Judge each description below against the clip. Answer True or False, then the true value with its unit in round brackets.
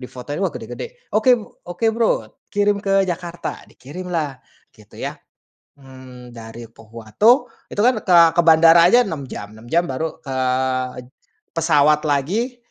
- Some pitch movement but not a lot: False (7.4 semitones)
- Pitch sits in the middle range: True (165 Hz)